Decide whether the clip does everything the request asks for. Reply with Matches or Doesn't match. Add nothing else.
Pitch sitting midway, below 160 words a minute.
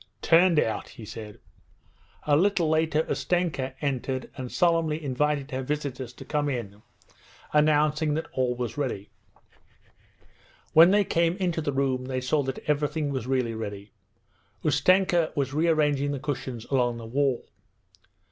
Matches